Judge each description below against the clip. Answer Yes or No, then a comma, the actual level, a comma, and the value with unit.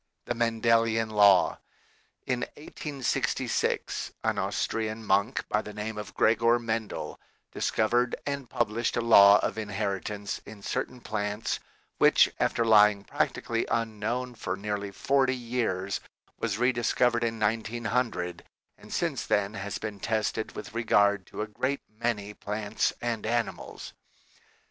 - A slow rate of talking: Yes, slow, 125 wpm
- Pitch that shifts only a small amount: Yes, narrow, 2.3 semitones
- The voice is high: No, low, 110 Hz